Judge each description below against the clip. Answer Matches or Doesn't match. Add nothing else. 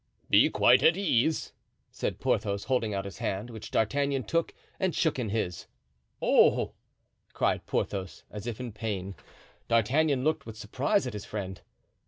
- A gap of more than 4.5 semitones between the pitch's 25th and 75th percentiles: Matches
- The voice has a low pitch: Matches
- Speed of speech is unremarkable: Matches